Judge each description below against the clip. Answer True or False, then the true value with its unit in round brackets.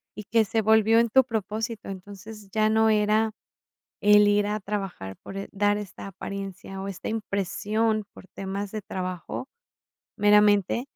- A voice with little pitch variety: True (1.9 semitones)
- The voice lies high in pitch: True (210 Hz)